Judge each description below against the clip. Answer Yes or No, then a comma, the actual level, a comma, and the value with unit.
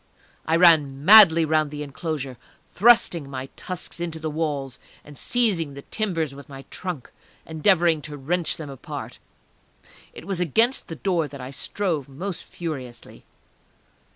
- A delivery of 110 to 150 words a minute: Yes, average, 145 wpm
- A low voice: No, medium, 160 Hz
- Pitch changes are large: No, average, 3.9 semitones